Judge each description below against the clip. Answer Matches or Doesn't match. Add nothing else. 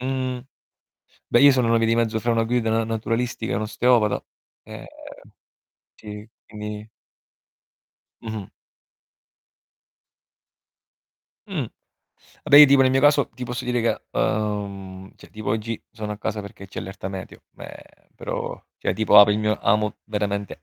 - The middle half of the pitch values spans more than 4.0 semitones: Doesn't match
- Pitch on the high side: Doesn't match